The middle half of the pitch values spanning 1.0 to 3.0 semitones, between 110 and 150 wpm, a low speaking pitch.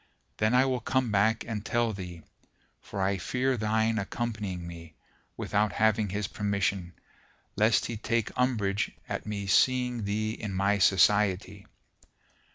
Yes: narrow, 2.5 semitones; average, 140 wpm; low, 105 Hz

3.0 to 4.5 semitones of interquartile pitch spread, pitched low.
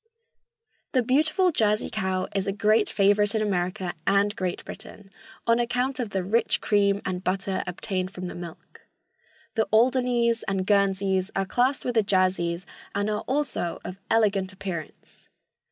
No: average, 3.3 semitones; high, 200 Hz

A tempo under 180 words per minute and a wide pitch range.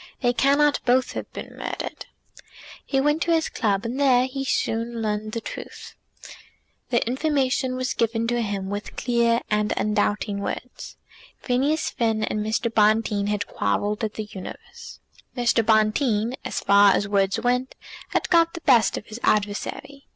No: average, 160 wpm; average, 3.5 semitones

